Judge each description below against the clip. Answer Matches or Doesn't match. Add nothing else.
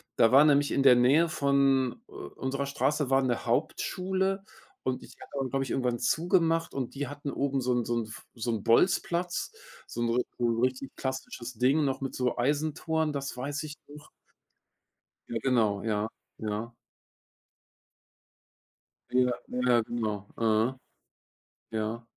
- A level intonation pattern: Doesn't match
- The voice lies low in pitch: Matches